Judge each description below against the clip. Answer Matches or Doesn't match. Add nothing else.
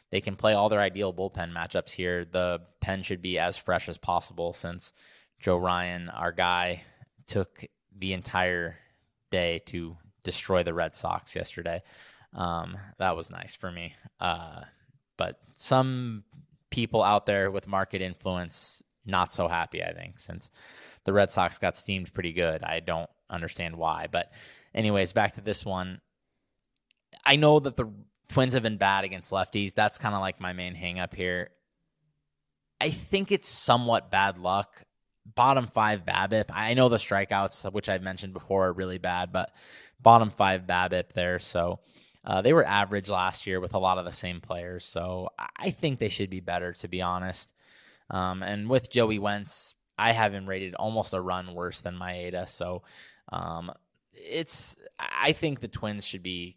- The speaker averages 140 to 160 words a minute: Doesn't match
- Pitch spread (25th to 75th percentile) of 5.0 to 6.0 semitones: Doesn't match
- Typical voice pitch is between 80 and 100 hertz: Matches